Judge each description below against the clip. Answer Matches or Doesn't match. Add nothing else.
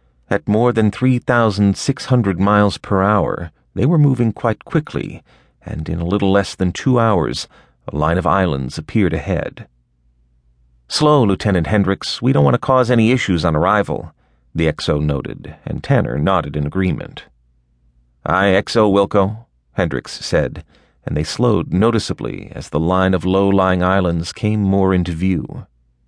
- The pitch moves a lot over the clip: Matches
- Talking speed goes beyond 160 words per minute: Doesn't match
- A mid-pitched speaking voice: Doesn't match